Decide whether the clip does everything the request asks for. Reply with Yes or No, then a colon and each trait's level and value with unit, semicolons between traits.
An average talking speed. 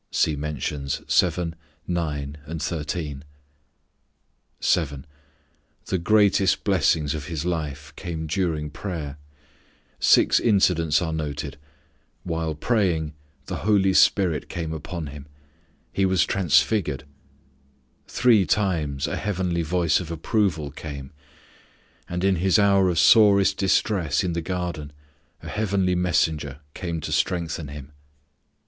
No: slow, 115 wpm